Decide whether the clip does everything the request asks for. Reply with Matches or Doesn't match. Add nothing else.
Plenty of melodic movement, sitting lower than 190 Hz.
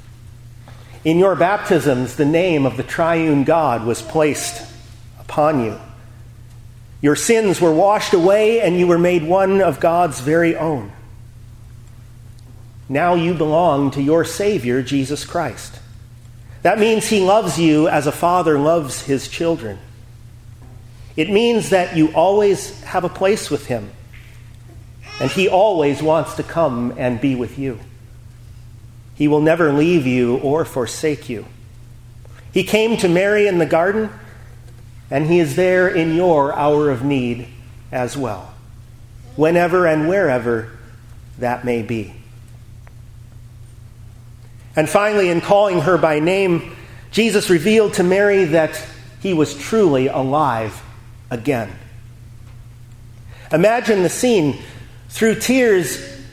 Matches